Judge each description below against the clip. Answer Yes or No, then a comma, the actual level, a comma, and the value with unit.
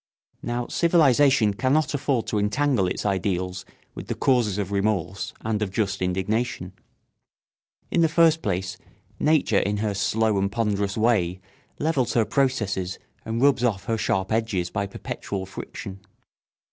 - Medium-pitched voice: No, low, 105 Hz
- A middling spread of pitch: Yes, average, 4.4 semitones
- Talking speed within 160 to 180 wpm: No, average, 145 wpm